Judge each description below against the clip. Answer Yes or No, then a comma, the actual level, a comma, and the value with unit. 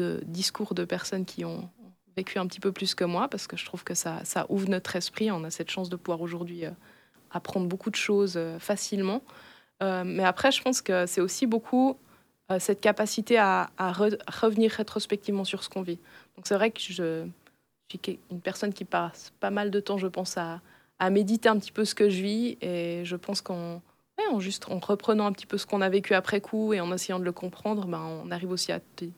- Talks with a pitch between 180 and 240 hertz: Yes, high, 190 Hz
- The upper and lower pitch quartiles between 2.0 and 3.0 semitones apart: Yes, narrow, 2.6 semitones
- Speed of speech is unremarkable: No, fast, 235 wpm